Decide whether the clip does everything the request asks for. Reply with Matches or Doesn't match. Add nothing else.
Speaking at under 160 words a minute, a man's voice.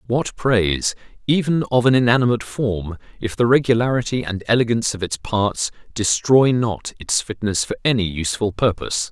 Matches